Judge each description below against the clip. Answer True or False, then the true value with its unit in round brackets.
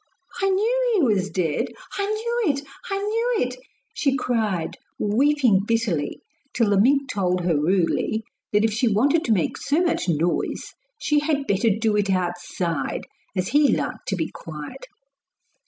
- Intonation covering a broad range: True (8.2 semitones)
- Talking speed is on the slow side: False (160 wpm)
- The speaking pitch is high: True (225 Hz)